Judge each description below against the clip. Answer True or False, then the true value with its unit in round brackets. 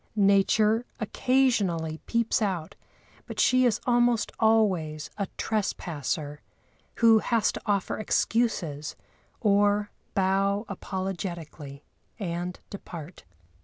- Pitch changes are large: False (4.5 semitones)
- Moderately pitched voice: False (200 Hz)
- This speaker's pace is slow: True (90 wpm)